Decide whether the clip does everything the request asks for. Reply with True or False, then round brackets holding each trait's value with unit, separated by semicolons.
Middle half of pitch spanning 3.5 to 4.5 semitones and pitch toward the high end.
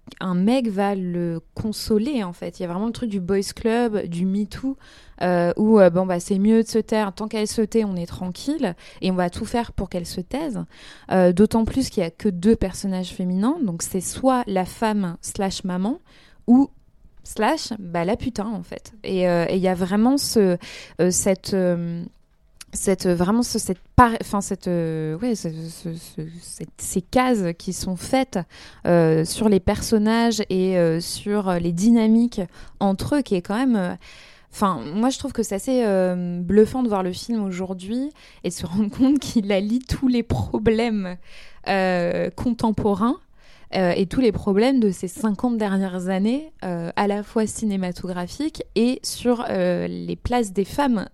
True (4.0 semitones; 200 Hz)